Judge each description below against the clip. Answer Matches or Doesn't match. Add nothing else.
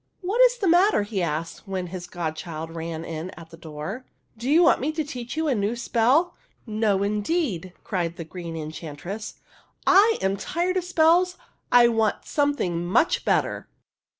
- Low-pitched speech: Doesn't match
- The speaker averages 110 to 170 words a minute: Doesn't match